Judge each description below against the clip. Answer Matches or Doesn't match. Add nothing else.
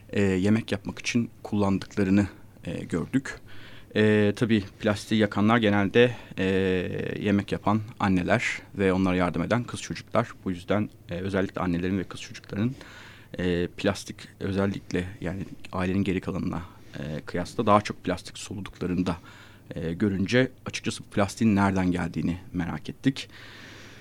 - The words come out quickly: Doesn't match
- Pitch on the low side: Matches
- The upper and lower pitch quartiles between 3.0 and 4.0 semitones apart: Doesn't match